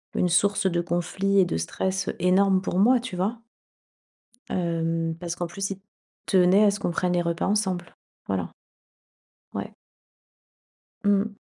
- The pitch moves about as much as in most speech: No, narrow, 2.3 semitones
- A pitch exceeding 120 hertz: Yes, medium, 185 Hz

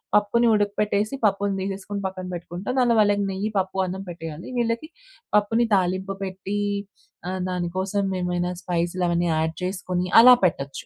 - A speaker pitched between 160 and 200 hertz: Yes, high, 190 Hz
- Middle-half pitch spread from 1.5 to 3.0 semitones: Yes, narrow, 2.5 semitones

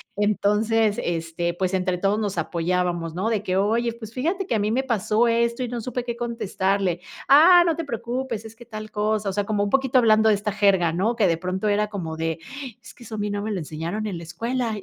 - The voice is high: Yes, high, 210 Hz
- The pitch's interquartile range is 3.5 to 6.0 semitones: Yes, average, 3.8 semitones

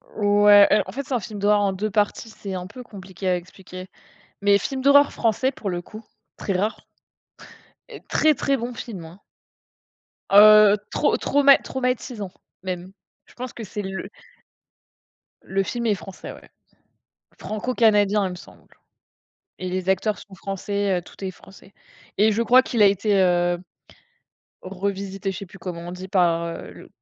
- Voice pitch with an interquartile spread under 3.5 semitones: Yes, average, 2.9 semitones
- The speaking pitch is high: Yes, high, 200 Hz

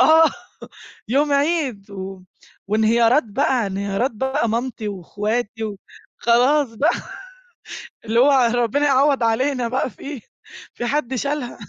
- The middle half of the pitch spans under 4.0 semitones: No, average, 4.3 semitones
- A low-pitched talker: No, high, 240 Hz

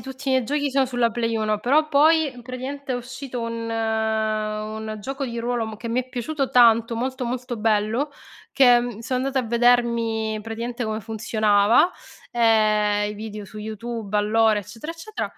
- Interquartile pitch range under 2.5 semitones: No, average, 2.8 semitones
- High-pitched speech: Yes, high, 230 Hz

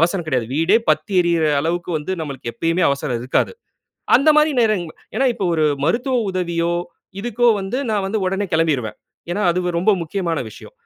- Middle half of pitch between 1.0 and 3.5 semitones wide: No, average, 4.3 semitones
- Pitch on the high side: No, medium, 175 Hz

